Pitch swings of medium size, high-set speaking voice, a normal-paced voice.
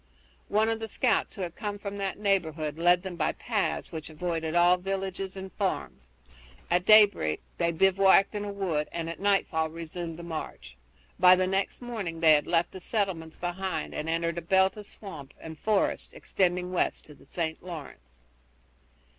No: average, 3.2 semitones; medium, 180 Hz; average, 180 wpm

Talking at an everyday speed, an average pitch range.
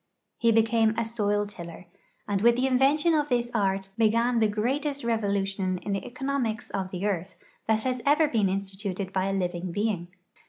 Yes: average, 185 wpm; average, 3.7 semitones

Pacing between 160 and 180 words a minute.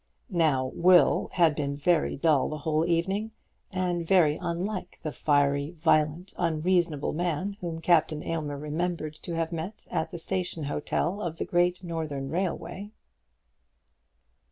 No: slow, 135 wpm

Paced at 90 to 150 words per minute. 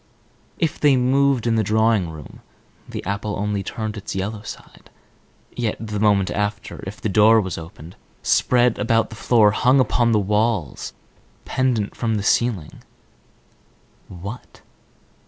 Yes: average, 140 wpm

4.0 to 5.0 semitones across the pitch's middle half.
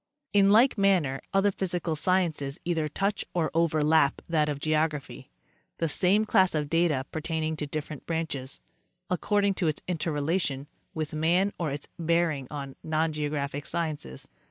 No: average, 3.1 semitones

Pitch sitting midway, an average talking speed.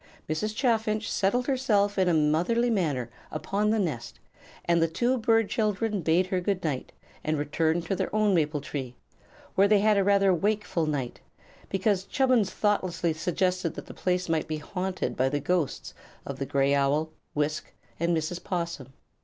Yes: medium, 180 Hz; average, 170 wpm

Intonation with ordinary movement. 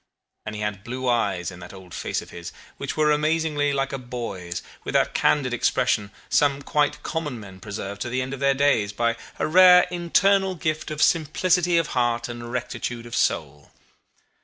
No: wide, 6.5 semitones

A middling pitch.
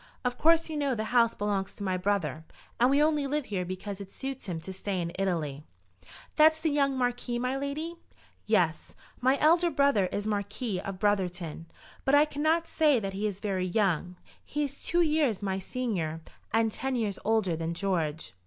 No: high, 215 Hz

